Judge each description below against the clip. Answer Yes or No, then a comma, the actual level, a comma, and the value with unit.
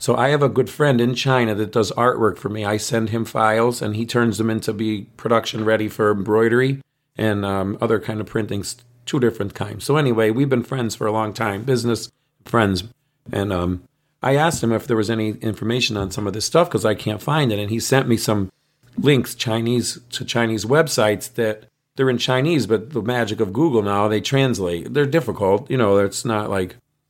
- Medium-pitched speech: No, low, 115 Hz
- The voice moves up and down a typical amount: Yes, average, 3.2 semitones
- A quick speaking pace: Yes, fast, 215 wpm